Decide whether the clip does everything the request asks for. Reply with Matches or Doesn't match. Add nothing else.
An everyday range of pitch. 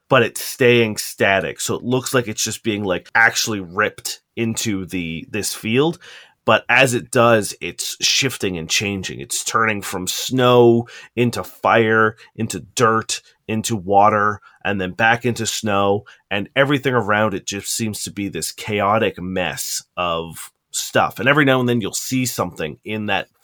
Matches